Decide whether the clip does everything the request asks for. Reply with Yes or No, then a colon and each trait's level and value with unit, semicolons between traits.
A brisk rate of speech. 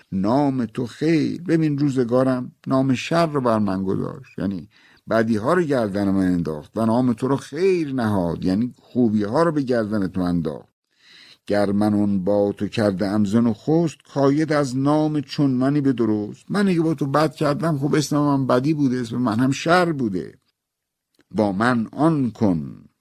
Yes: fast, 175 wpm